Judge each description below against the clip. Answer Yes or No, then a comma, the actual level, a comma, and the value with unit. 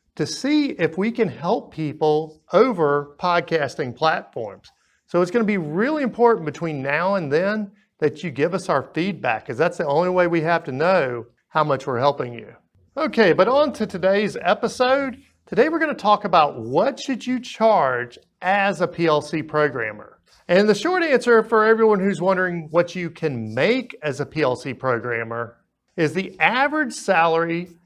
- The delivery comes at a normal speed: Yes, average, 175 wpm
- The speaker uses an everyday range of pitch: No, wide, 6.5 semitones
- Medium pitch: Yes, medium, 180 Hz